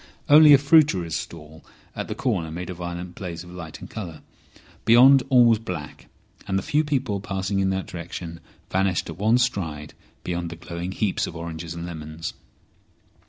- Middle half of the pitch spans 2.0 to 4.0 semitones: No, average, 4.6 semitones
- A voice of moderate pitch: No, very low, 90 Hz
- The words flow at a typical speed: Yes, average, 175 wpm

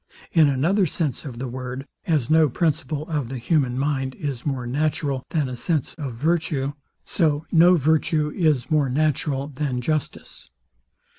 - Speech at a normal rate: Yes, average, 155 wpm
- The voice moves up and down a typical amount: Yes, average, 3.0 semitones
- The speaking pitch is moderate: Yes, medium, 145 Hz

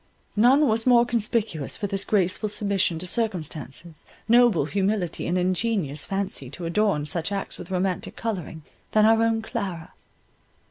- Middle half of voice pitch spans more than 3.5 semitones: Yes, average, 4.7 semitones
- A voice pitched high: Yes, high, 195 Hz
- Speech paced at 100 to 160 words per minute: Yes, average, 145 wpm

